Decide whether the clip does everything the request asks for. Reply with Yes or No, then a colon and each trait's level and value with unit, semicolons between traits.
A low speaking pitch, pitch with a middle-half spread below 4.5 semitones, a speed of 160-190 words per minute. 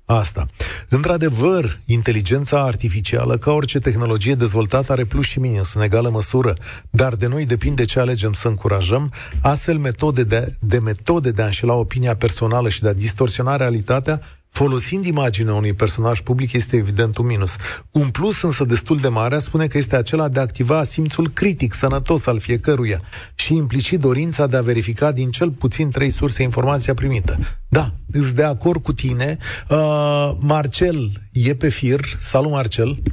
Yes: low, 125 Hz; average, 4.1 semitones; average, 165 wpm